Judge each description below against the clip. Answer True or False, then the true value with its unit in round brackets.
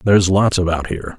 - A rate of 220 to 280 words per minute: False (205 wpm)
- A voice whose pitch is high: False (95 Hz)